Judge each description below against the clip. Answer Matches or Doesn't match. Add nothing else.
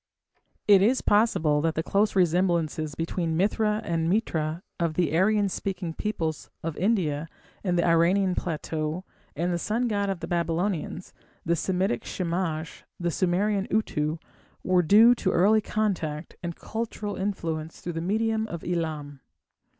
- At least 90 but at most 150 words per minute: Matches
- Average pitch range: Matches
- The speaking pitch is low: Doesn't match